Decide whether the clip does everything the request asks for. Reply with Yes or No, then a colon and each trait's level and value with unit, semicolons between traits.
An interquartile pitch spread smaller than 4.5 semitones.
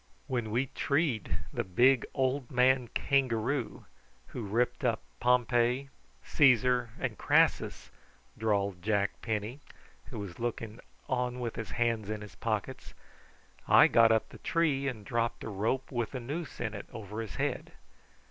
Yes: average, 3.0 semitones